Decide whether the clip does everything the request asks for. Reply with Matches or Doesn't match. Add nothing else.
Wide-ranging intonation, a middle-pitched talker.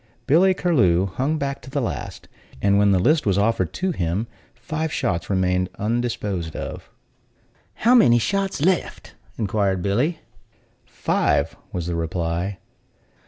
Doesn't match